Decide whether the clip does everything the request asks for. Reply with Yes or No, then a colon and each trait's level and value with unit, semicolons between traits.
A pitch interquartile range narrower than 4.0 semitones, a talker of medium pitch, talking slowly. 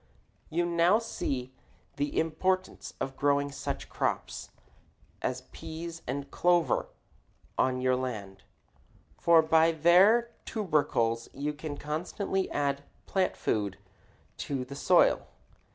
No: average, 4.4 semitones; medium, 150 Hz; slow, 110 wpm